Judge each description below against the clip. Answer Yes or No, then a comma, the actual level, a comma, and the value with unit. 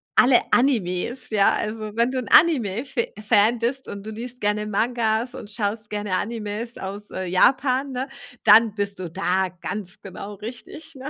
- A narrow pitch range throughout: No, average, 3.4 semitones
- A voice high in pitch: Yes, high, 220 Hz